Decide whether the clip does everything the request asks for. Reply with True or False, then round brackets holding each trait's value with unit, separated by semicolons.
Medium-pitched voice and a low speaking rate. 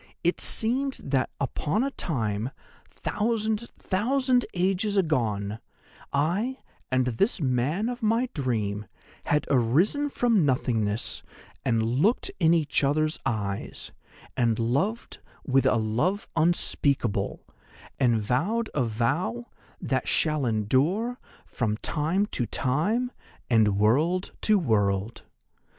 True (145 Hz; 110 wpm)